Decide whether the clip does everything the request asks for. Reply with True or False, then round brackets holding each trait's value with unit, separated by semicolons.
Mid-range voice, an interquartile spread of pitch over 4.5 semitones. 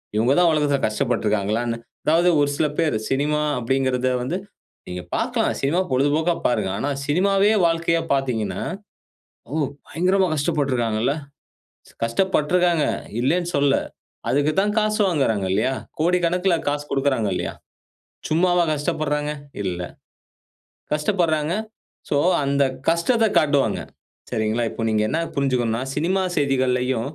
True (145 Hz; 5.2 semitones)